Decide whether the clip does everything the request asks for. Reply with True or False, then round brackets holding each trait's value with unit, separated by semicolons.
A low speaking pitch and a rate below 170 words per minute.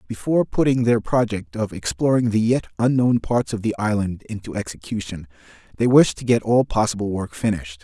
False (110 Hz; 175 wpm)